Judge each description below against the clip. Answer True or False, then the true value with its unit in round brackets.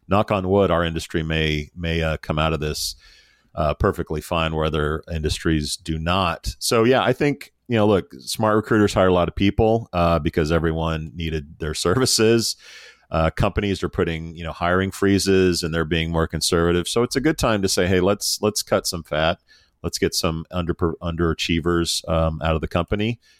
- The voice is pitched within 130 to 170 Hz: False (85 Hz)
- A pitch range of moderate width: True (3.6 semitones)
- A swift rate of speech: False (195 wpm)